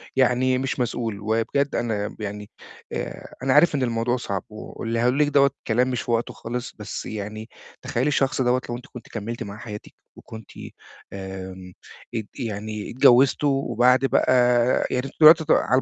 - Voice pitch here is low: Yes, low, 120 Hz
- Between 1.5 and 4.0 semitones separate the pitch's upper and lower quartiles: Yes, average, 3.2 semitones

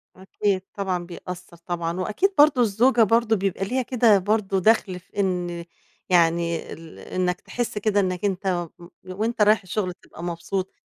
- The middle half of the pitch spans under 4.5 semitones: Yes, average, 3.3 semitones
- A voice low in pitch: No, high, 190 Hz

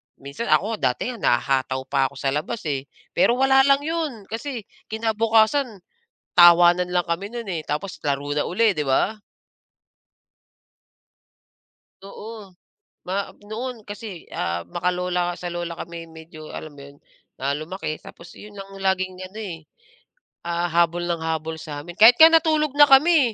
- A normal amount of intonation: No, wide, 5.9 semitones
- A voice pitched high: No, medium, 180 Hz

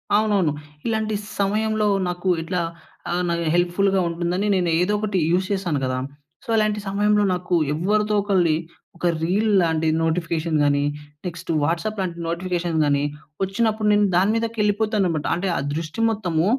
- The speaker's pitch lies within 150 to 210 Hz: Yes, medium, 185 Hz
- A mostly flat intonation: No, average, 3.7 semitones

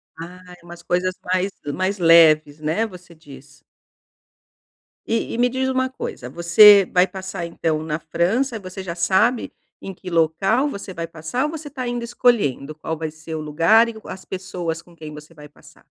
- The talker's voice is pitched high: No, medium, 180 Hz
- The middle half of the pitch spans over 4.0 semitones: Yes, average, 4.9 semitones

